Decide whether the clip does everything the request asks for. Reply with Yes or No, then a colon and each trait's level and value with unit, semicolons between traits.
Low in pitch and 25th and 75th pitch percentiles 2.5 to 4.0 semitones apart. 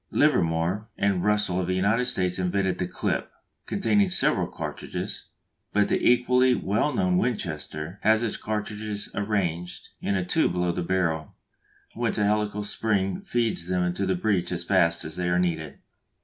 Yes: low, 100 Hz; average, 3.6 semitones